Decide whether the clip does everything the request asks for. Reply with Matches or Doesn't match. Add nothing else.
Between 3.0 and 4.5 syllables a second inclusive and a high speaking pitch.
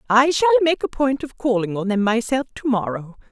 Doesn't match